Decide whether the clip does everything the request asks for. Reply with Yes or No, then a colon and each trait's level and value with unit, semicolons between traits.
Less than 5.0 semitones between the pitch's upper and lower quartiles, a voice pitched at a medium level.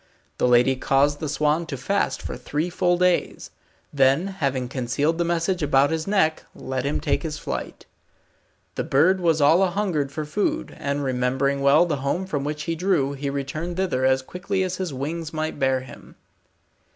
Yes: average, 4.1 semitones; medium, 150 Hz